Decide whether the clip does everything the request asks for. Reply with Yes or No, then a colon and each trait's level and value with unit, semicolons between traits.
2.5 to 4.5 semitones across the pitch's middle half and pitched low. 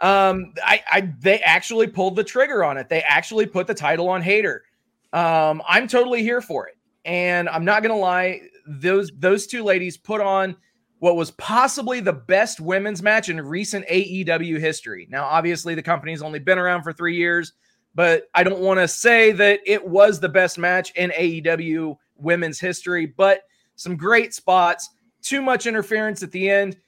No: average, 3.5 semitones; medium, 185 Hz